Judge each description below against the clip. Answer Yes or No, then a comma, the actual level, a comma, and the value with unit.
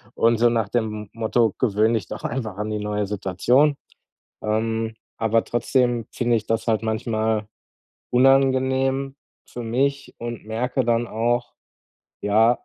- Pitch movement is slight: Yes, narrow, 2.1 semitones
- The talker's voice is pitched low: Yes, low, 115 Hz